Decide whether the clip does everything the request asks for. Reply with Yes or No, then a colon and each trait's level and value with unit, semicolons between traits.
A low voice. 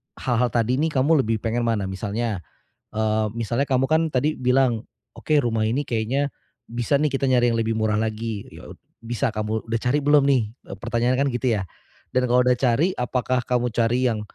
Yes: low, 120 Hz